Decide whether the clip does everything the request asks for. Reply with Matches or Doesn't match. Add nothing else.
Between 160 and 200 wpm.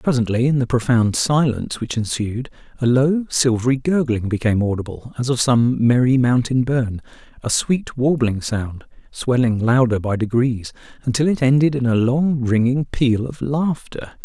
Doesn't match